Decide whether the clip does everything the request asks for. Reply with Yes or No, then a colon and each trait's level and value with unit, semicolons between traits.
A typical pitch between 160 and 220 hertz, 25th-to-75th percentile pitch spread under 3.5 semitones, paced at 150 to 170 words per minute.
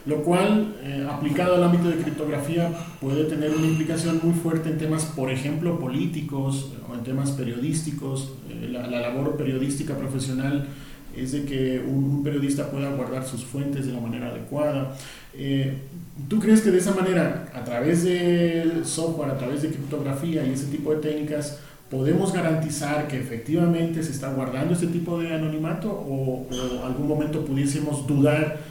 No: medium, 145 Hz; average, 3.1 semitones; average, 165 wpm